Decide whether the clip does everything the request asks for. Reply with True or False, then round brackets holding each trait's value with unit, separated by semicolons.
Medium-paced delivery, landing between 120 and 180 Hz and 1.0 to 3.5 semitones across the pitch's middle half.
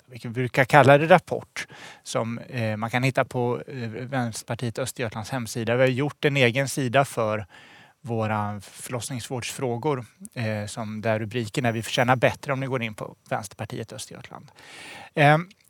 True (150 wpm; 125 Hz; 2.8 semitones)